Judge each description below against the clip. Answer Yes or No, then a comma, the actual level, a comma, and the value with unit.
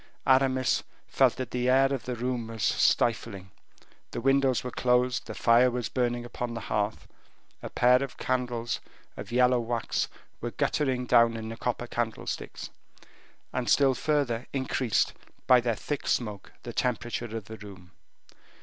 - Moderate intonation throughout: No, narrow, 1.8 semitones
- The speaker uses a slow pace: No, average, 155 wpm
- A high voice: No, low, 120 Hz